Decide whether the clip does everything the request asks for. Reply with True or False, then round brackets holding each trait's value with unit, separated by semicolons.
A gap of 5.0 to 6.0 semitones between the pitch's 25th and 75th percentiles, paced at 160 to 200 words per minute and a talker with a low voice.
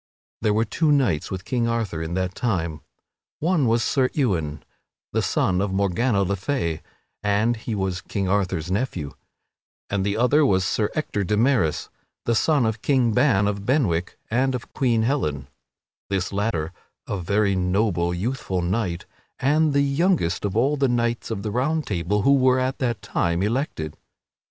True (5.6 semitones; 170 wpm; 105 Hz)